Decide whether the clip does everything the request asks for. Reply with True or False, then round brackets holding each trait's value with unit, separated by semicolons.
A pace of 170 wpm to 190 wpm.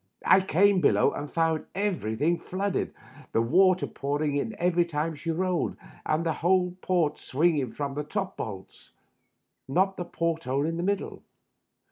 False (160 wpm)